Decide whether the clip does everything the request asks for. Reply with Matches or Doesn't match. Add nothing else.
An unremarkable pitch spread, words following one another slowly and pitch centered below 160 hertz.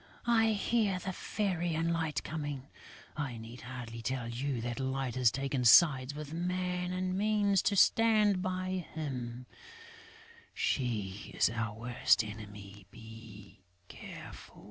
Doesn't match